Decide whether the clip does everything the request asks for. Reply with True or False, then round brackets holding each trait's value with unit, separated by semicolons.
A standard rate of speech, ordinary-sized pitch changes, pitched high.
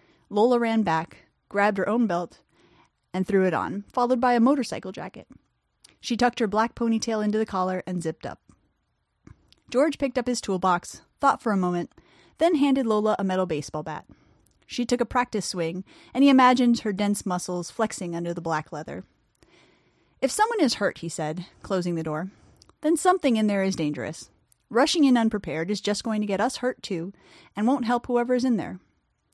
False (190 wpm; 5.8 semitones; 210 Hz)